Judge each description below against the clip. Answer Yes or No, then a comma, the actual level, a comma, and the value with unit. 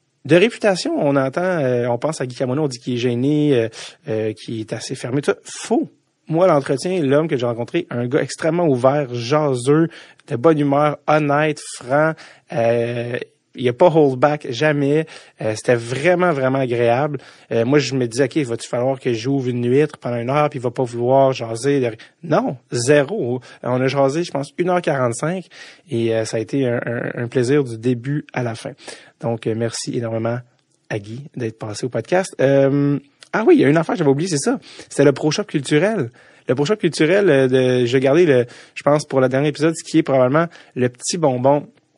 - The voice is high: No, low, 135 Hz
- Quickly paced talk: Yes, fast, 210 wpm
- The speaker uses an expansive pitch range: No, average, 3.7 semitones